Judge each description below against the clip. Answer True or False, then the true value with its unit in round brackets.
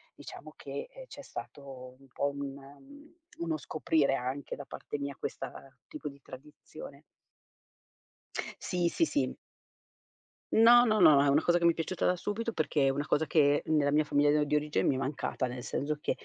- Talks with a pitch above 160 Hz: False (150 Hz)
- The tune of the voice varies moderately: True (3.4 semitones)